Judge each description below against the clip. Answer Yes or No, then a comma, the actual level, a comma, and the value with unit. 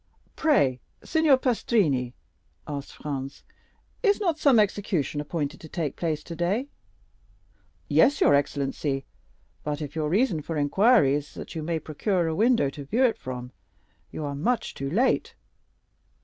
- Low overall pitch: No, medium, 160 Hz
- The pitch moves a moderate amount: No, wide, 7.8 semitones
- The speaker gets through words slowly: No, average, 145 wpm